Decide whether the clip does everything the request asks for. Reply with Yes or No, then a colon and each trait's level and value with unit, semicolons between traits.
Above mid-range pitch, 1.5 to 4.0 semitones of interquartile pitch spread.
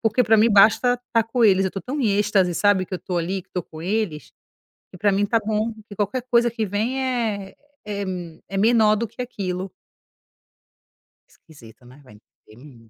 Yes: high, 205 Hz; average, 3.7 semitones